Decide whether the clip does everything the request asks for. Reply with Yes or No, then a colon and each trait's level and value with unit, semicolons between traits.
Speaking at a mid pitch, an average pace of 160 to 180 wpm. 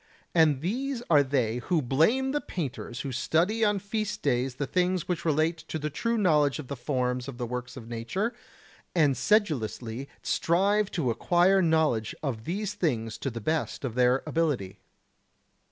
Yes: medium, 150 Hz; average, 170 wpm